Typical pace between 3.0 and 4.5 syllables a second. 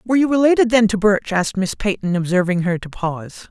No: 6.1 syllables/s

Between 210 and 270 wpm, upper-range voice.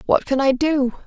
Yes: fast, 225 wpm; very high, 275 Hz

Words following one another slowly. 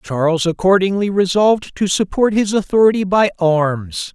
Yes: slow, 130 wpm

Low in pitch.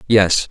Yes: low, 100 Hz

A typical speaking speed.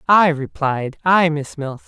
Yes: average, 160 wpm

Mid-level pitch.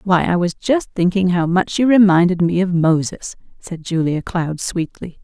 Yes: medium, 180 Hz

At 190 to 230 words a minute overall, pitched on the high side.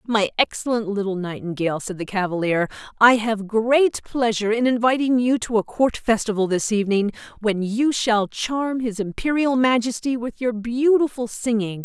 No: average, 155 wpm; high, 225 Hz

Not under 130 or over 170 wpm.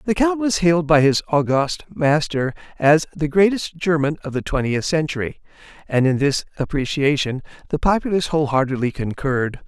Yes: average, 150 wpm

